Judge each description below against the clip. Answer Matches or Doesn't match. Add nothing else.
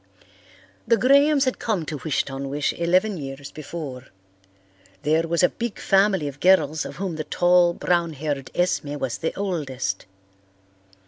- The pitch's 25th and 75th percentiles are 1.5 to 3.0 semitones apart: Doesn't match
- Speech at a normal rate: Matches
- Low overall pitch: Doesn't match